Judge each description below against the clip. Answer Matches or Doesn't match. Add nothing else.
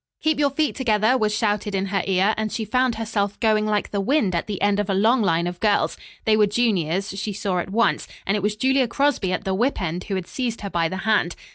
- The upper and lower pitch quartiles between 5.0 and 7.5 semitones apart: Doesn't match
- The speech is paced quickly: Matches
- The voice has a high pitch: Matches